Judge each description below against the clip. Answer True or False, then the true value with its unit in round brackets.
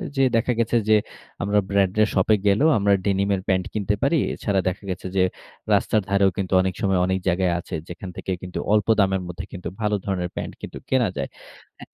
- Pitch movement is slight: True (2.1 semitones)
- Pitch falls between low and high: False (100 Hz)